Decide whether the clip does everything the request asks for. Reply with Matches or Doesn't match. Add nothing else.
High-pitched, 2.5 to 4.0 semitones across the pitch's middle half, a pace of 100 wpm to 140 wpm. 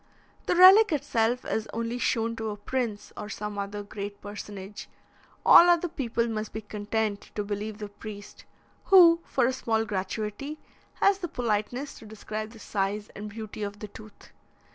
Doesn't match